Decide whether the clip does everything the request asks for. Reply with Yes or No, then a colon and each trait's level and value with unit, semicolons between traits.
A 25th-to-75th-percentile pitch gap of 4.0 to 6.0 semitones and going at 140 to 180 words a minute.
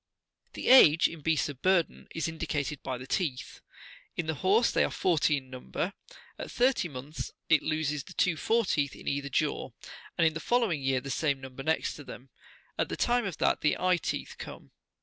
No: average, 4.6 semitones; average, 200 wpm